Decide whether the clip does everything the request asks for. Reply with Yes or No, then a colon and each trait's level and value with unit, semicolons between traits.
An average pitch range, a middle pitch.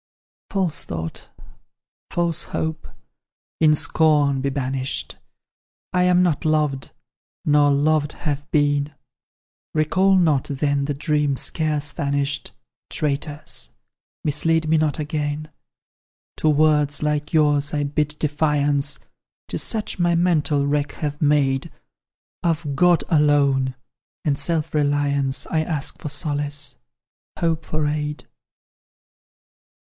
No: narrow, 1.6 semitones; medium, 150 Hz